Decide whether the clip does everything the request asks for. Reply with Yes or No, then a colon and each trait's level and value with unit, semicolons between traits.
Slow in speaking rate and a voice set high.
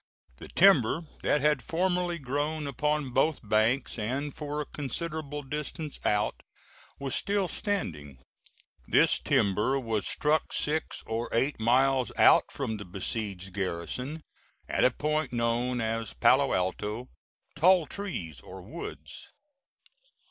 No: slow, 125 wpm; low, 135 Hz